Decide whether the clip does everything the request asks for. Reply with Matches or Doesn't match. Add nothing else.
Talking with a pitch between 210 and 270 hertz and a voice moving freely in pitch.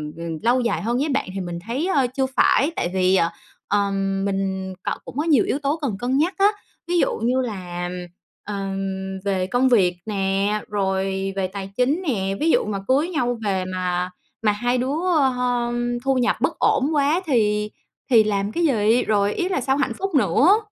Matches